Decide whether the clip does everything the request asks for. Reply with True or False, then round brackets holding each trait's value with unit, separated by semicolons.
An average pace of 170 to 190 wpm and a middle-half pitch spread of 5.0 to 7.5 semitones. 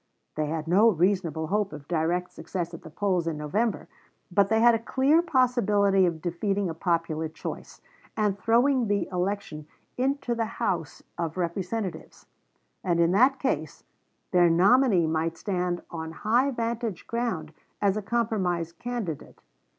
False (150 wpm; 5.4 semitones)